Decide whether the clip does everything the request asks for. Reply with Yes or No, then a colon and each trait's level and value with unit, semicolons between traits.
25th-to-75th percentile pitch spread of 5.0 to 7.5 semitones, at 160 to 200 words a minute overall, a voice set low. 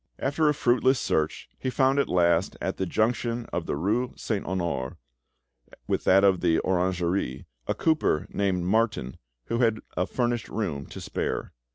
Yes: wide, 5.6 semitones; average, 165 wpm; low, 100 Hz